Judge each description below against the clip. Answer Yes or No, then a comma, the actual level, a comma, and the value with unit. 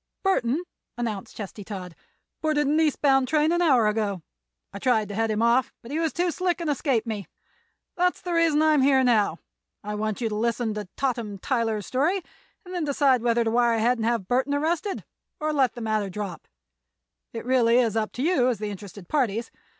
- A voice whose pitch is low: No, high, 240 Hz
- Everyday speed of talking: No, fast, 210 wpm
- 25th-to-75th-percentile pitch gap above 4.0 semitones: Yes, wide, 5.5 semitones